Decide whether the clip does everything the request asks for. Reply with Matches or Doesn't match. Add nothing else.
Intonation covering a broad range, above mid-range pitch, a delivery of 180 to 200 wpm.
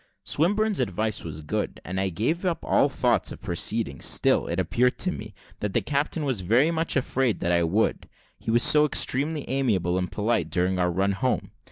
Doesn't match